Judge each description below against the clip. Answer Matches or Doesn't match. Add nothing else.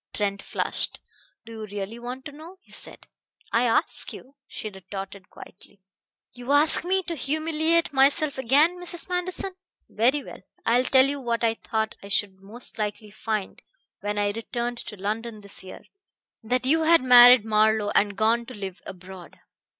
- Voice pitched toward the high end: Matches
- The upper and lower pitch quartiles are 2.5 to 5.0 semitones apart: Doesn't match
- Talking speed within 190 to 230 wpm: Doesn't match